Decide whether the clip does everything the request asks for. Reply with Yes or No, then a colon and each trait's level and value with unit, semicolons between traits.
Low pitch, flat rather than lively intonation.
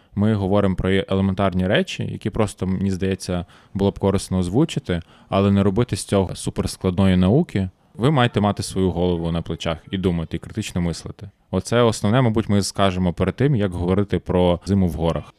Yes: very low, 95 Hz; narrow, 2.2 semitones